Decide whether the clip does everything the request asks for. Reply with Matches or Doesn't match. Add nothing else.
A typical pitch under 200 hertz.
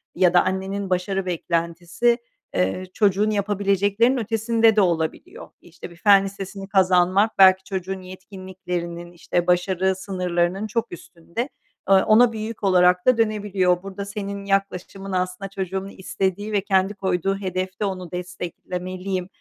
Matches